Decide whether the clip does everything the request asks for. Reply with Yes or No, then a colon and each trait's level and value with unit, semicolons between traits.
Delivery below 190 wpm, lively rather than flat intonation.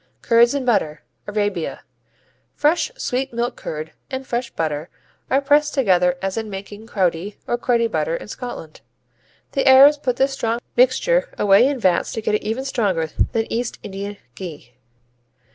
Yes: average, 160 wpm; wide, 5.8 semitones